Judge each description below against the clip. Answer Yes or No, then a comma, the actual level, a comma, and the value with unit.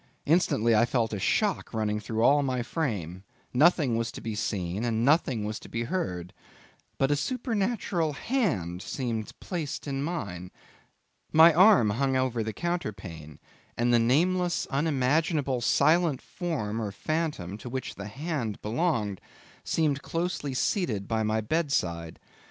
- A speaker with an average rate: Yes, average, 145 wpm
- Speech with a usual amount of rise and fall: No, wide, 7.1 semitones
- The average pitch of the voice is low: Yes, low, 125 Hz